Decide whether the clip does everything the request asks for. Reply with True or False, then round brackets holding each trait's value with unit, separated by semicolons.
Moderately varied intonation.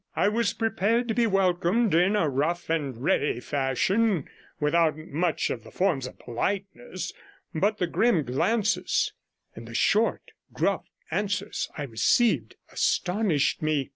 False (6.4 semitones)